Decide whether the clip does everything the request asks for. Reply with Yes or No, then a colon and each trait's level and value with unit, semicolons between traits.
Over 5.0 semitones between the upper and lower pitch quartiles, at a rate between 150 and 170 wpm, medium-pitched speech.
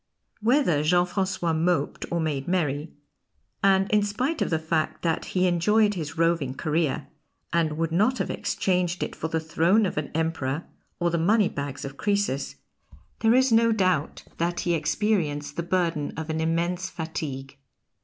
No: average, 3.4 semitones; average, 165 wpm; medium, 170 Hz